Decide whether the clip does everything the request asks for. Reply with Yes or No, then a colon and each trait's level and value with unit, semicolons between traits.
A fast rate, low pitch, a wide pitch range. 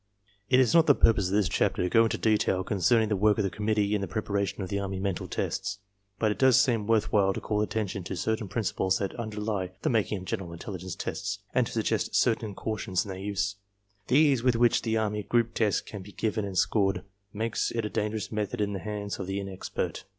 No: fast, 240 wpm; low, 105 Hz; narrow, 2.4 semitones